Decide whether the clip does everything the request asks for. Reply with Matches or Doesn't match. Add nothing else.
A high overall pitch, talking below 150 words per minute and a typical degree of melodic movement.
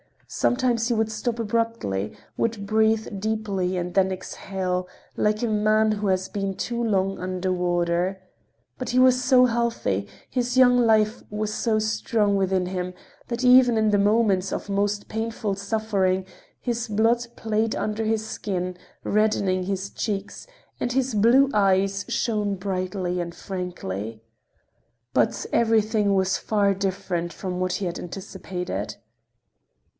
Matches